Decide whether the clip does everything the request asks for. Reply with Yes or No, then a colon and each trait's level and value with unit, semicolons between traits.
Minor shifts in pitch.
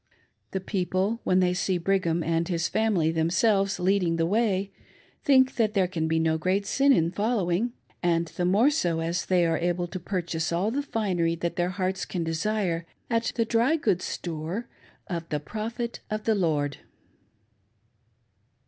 No: average, 4.3 semitones